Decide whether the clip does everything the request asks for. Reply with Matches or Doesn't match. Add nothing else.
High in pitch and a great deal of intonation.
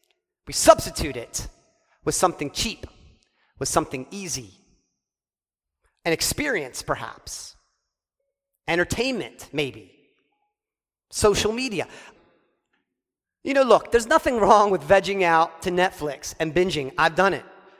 Matches